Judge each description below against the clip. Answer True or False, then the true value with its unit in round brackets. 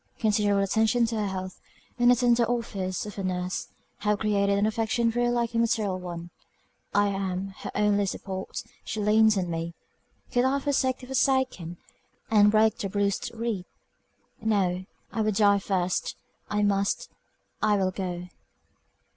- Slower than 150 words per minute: False (155 wpm)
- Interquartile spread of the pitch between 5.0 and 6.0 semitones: False (3.2 semitones)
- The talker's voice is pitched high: True (205 Hz)